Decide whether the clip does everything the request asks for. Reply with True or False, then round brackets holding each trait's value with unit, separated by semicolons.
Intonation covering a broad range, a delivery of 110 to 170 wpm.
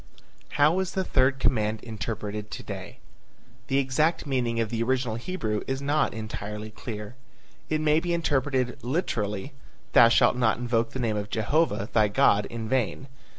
False (4.3 semitones; 160 wpm)